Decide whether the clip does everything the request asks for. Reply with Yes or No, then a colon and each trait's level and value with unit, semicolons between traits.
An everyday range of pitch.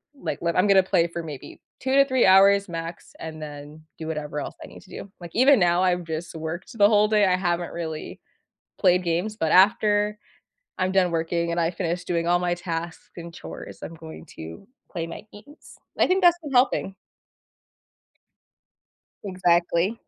Yes: average, 3.3 semitones